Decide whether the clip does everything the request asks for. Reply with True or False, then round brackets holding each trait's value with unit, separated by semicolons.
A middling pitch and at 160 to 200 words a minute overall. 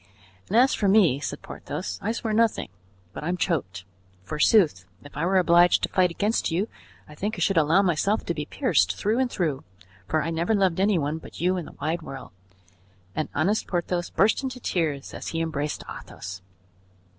True (175 Hz; 190 wpm)